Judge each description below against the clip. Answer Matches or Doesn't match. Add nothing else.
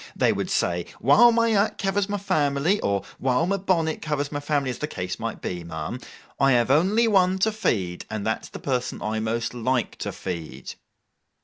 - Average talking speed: Matches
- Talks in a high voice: Doesn't match